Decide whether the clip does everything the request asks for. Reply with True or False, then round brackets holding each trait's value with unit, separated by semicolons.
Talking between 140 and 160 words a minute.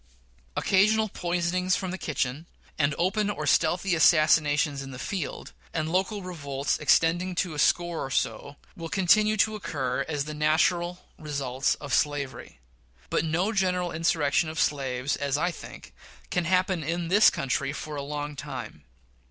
True (155 wpm)